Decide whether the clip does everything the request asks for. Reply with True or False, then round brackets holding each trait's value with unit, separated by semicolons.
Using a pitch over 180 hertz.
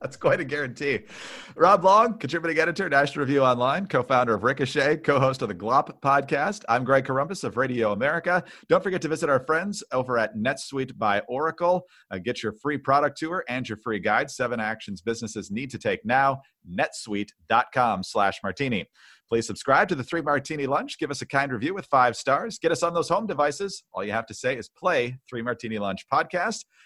False (140 Hz)